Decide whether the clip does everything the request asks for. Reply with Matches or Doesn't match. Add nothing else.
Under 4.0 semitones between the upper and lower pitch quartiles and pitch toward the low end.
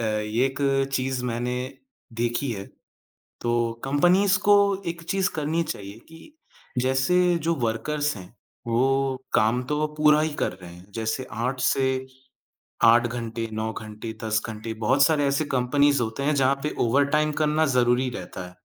Doesn't match